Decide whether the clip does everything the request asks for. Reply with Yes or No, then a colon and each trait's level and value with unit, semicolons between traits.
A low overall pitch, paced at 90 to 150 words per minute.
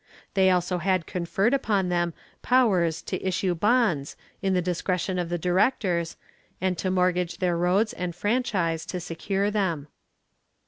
No: medium, 180 Hz; average, 145 wpm